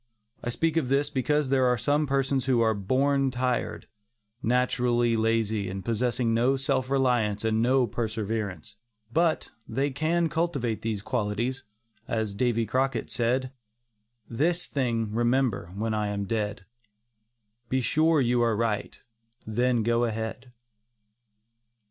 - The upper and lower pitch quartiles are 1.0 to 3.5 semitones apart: Yes, average, 3.1 semitones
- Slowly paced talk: Yes, slow, 130 wpm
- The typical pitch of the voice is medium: No, low, 120 Hz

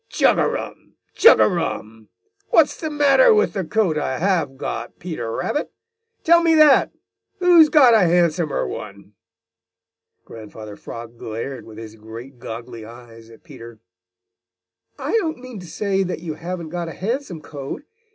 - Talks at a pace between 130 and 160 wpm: Yes, average, 155 wpm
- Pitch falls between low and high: Yes, medium, 160 Hz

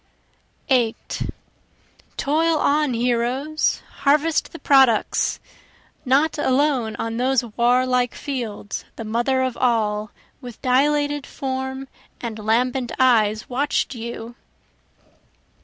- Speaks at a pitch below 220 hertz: No, very high, 255 Hz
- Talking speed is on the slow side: Yes, slow, 95 wpm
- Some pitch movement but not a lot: Yes, average, 3.0 semitones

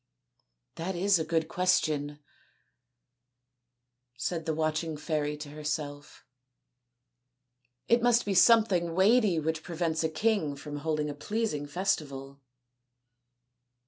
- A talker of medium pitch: Yes, medium, 155 Hz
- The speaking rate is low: Yes, slow, 115 wpm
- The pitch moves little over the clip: No, average, 3.7 semitones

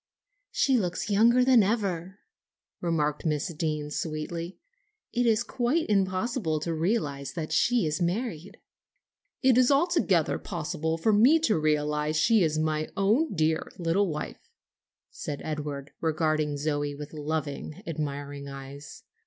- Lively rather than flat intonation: Yes, wide, 5.7 semitones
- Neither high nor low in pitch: Yes, medium, 165 Hz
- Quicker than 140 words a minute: No, slow, 135 wpm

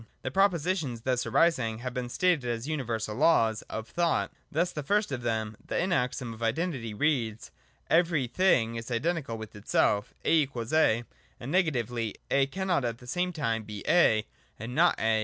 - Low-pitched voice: Yes, low, 125 Hz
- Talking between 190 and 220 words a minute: No, average, 165 wpm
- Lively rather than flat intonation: Yes, wide, 6.3 semitones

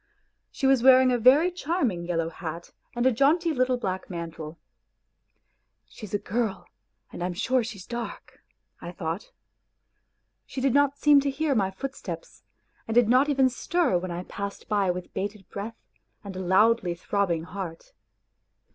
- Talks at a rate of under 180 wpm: Yes, average, 165 wpm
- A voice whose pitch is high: Yes, high, 215 Hz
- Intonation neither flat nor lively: No, wide, 6.4 semitones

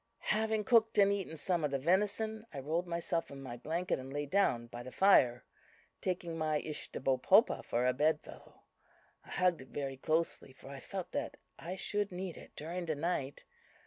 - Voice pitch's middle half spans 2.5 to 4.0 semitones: No, wide, 5.6 semitones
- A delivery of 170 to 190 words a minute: Yes, average, 185 wpm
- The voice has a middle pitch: Yes, medium, 165 Hz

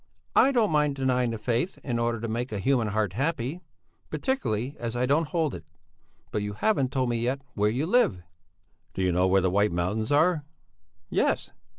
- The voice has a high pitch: No, low, 120 Hz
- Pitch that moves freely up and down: Yes, wide, 5.7 semitones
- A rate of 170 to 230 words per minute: Yes, average, 195 wpm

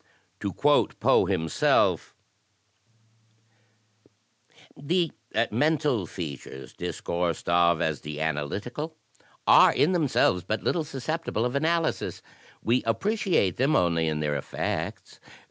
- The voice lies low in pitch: Yes, low, 110 Hz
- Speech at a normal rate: No, slow, 110 wpm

